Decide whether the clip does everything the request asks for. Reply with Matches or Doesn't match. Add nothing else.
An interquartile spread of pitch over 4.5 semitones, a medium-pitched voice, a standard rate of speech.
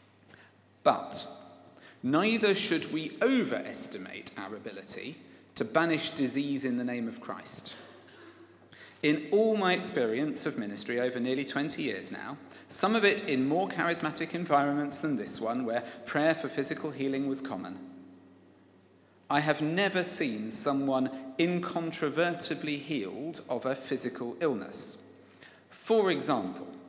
Doesn't match